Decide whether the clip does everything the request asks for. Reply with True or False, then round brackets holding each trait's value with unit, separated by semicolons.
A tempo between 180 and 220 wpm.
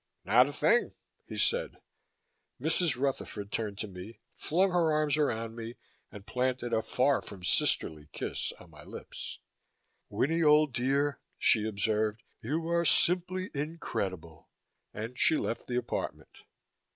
False (140 wpm)